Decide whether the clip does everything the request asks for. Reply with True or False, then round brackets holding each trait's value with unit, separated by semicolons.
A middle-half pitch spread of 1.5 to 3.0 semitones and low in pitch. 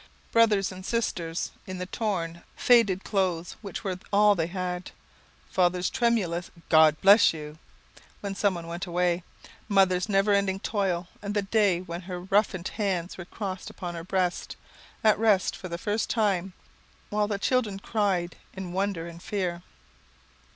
False (2.7 semitones; 190 Hz)